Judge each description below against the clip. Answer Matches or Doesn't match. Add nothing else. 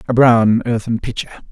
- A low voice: Matches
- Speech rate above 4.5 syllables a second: Matches